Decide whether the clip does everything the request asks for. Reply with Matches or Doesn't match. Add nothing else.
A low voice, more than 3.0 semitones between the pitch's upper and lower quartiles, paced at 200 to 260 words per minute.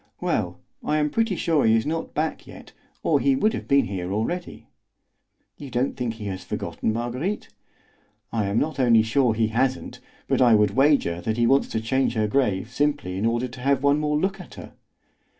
Matches